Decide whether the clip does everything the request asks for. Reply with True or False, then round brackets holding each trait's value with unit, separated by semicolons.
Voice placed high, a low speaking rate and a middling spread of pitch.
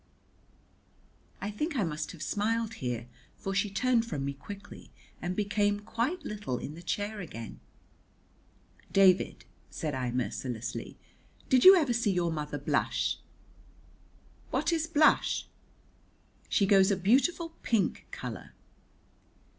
False (200 Hz; 125 wpm; 7.2 semitones)